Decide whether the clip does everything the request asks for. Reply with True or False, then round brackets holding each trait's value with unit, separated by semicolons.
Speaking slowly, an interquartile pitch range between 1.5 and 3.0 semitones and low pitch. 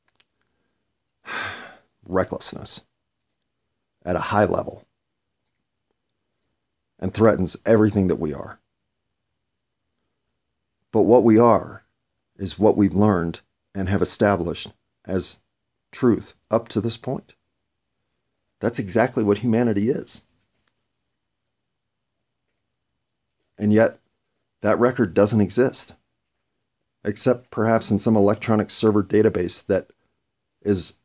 True (95 wpm; 2.7 semitones; 105 Hz)